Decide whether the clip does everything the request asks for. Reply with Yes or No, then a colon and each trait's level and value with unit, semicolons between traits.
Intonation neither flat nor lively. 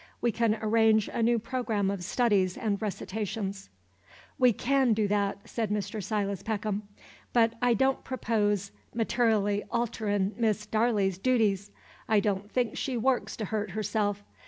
No: narrow, 2.3 semitones